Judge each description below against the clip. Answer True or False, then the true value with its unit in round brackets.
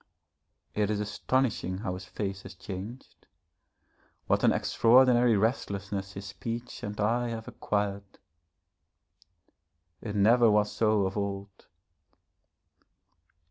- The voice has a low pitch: True (105 Hz)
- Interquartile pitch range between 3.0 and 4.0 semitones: False (2.6 semitones)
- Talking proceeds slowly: True (105 wpm)